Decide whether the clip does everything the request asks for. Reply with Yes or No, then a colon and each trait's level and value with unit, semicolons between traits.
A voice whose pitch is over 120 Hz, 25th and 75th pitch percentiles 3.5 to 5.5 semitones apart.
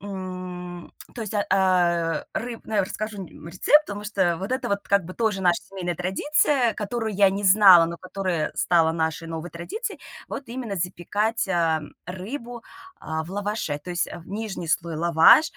Yes: high, 190 Hz; average, 3.8 semitones